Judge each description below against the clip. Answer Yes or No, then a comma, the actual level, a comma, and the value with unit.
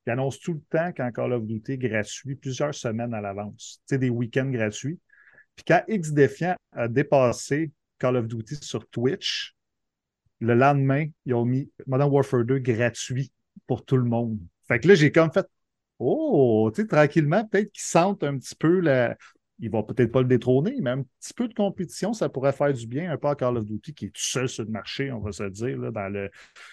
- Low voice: Yes, low, 130 Hz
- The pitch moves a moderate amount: Yes, average, 4.1 semitones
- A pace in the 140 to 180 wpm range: No, average, 210 wpm